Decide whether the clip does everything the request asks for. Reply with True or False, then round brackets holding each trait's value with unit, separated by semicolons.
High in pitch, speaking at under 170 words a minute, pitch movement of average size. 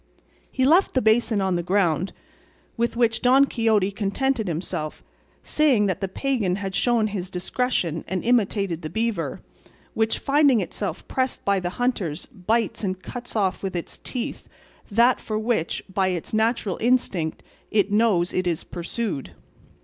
True (210 Hz; 155 wpm; 4.4 semitones)